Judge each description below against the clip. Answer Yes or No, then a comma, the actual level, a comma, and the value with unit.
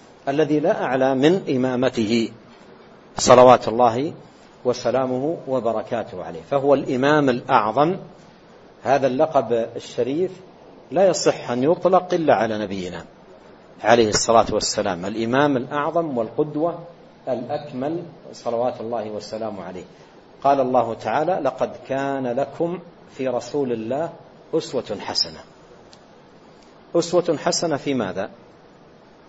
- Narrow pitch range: No, average, 5.1 semitones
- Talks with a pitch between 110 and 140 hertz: Yes, low, 135 Hz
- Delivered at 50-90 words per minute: No, average, 100 wpm